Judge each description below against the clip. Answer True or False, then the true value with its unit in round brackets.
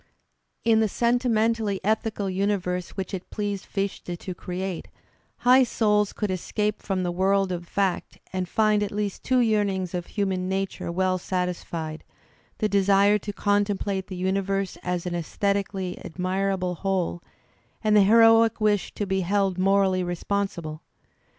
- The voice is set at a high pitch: True (195 Hz)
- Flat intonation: True (2.1 semitones)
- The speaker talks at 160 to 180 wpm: False (145 wpm)